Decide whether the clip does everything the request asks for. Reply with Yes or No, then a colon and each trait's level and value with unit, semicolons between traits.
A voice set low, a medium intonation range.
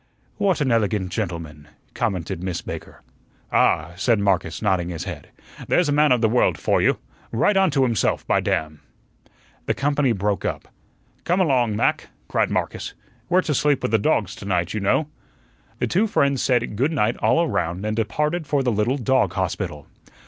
No: low, 115 Hz; wide, 7.2 semitones